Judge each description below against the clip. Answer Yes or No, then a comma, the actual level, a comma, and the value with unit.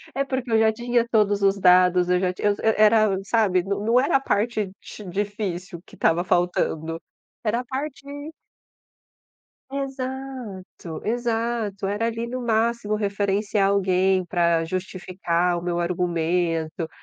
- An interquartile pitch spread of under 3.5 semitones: No, average, 4.3 semitones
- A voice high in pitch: Yes, high, 200 Hz